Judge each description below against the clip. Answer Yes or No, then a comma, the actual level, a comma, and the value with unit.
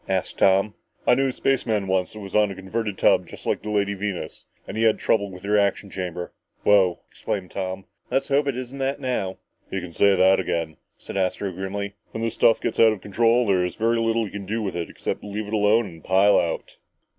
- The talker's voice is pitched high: No, low, 100 Hz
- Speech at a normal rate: No, fast, 225 wpm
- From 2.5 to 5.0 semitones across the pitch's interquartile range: Yes, average, 3.0 semitones